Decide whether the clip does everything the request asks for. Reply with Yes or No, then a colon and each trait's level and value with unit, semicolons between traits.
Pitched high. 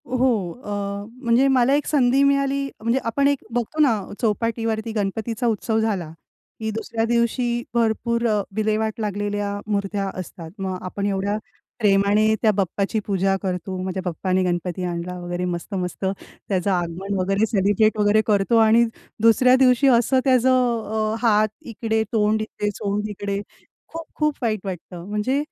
Yes: high, 215 Hz